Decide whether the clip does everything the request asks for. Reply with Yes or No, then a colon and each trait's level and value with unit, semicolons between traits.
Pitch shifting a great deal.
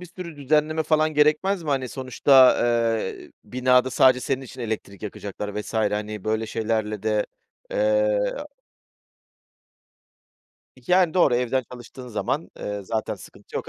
Yes: wide, 5.8 semitones